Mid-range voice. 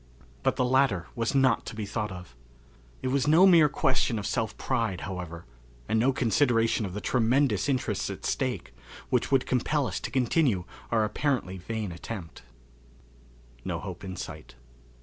No: low, 115 Hz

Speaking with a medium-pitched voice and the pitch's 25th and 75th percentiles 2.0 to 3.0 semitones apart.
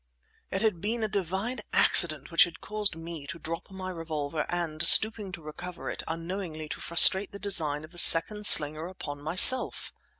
No: medium, 170 Hz; average, 3.9 semitones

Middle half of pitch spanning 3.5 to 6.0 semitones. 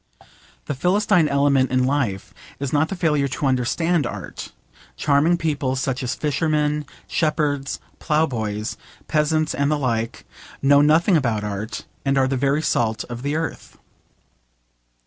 No: average, 3.1 semitones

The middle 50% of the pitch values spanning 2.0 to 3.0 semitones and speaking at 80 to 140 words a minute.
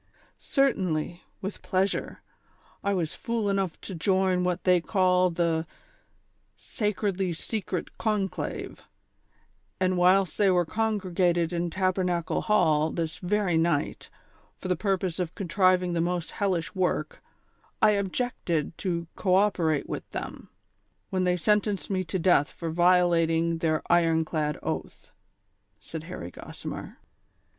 Yes: narrow, 2.5 semitones; slow, 135 wpm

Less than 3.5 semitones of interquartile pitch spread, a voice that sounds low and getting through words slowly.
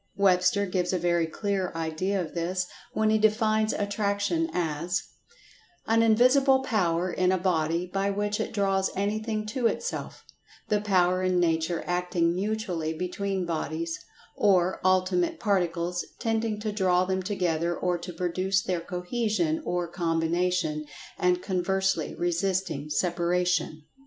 No: average, 2.8 semitones; medium, 185 Hz; slow, 130 wpm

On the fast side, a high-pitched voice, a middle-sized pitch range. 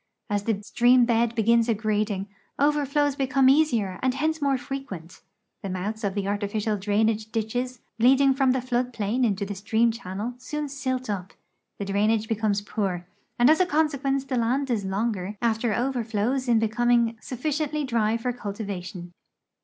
No: average, 165 wpm; high, 230 Hz; average, 4.0 semitones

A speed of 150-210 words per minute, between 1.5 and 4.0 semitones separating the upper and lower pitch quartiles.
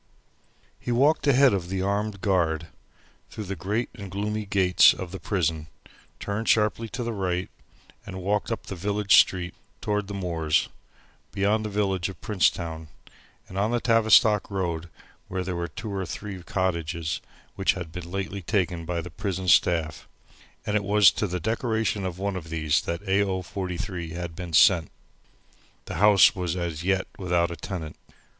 Yes: average, 170 wpm; average, 3.1 semitones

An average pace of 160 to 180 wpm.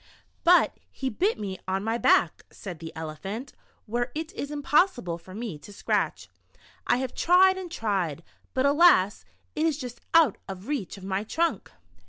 Yes: average, 175 wpm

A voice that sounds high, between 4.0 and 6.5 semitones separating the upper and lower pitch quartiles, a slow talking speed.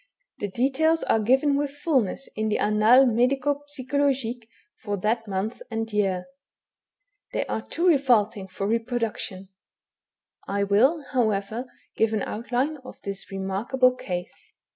Yes: high, 230 Hz; average, 4.5 semitones; slow, 130 wpm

